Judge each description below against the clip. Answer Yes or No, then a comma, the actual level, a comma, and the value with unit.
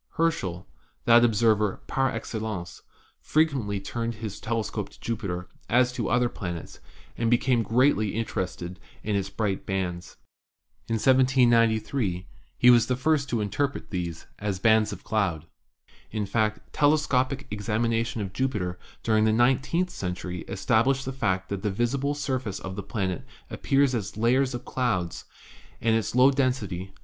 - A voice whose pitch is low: Yes, low, 115 Hz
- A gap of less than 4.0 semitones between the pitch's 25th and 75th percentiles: No, average, 4.5 semitones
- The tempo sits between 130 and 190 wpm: Yes, average, 150 wpm